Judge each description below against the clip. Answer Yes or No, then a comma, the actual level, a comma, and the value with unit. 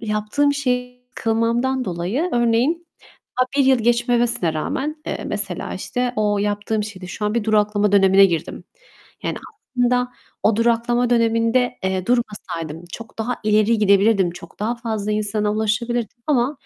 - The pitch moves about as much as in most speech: Yes, average, 3.0 semitones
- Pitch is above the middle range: Yes, high, 225 Hz